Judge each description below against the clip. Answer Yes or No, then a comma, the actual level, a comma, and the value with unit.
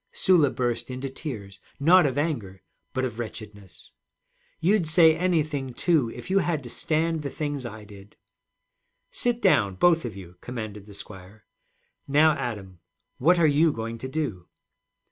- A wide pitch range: Yes, wide, 7.0 semitones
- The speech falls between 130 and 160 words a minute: Yes, average, 155 wpm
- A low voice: Yes, low, 130 Hz